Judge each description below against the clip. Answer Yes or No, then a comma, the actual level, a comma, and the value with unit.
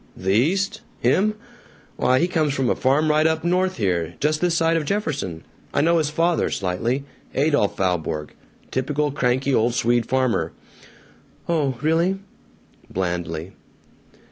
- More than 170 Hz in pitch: No, medium, 140 Hz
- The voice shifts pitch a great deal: Yes, wide, 6.6 semitones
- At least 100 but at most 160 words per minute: Yes, average, 140 wpm